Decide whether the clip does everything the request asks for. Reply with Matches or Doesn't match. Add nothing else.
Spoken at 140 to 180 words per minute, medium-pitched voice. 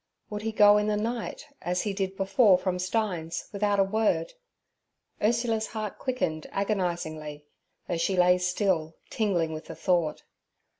Doesn't match